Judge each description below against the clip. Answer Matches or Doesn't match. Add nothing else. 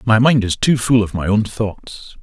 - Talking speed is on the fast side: Matches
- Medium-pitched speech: Doesn't match